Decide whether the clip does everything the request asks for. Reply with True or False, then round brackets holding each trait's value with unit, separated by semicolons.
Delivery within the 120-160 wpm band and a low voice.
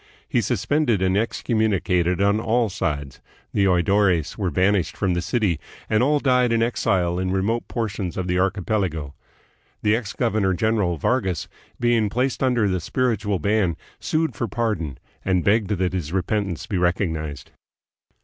True (150 wpm; 100 Hz)